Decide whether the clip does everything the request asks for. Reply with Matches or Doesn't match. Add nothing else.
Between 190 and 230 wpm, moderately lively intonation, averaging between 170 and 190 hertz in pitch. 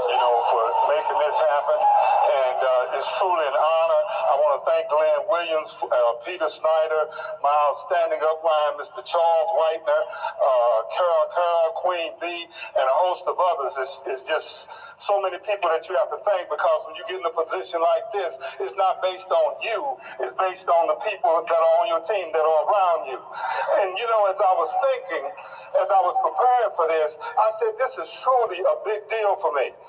Doesn't match